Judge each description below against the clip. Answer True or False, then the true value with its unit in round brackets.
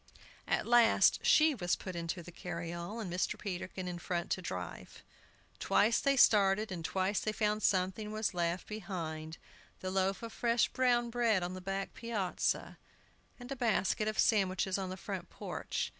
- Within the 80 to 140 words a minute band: False (170 wpm)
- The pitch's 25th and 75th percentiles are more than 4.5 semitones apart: False (3.5 semitones)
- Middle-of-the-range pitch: False (195 Hz)